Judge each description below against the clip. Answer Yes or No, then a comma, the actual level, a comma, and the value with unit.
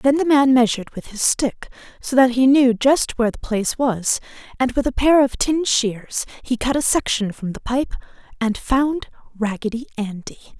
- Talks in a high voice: Yes, high, 245 Hz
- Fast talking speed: No, average, 195 wpm